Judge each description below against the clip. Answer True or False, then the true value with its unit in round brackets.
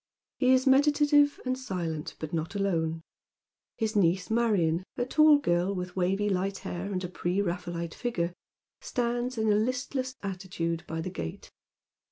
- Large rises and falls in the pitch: True (6.2 semitones)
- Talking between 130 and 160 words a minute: True (155 wpm)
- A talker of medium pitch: False (195 Hz)